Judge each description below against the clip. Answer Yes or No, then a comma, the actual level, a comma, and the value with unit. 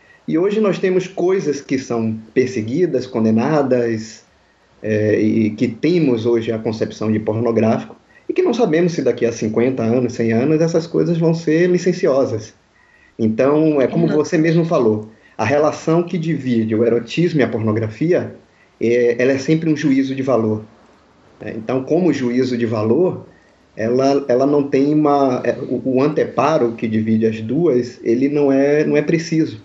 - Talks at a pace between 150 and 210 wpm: Yes, average, 165 wpm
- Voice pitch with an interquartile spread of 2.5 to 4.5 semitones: No, wide, 5.4 semitones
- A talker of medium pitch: No, low, 130 Hz